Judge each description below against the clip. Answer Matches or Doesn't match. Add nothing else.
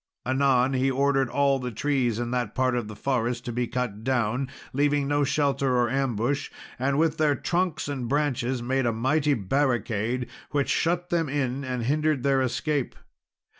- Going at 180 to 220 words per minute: Doesn't match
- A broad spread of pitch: Doesn't match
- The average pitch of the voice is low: Matches